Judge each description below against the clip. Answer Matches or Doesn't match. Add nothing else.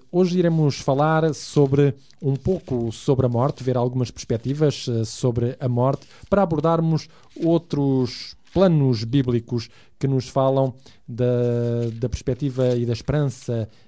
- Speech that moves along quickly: Doesn't match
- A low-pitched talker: Matches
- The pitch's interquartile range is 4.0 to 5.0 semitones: Doesn't match